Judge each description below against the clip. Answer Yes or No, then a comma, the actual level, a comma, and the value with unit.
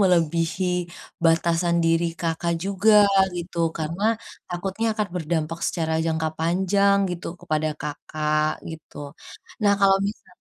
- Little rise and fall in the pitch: No, average, 3.0 semitones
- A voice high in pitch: No, medium, 170 Hz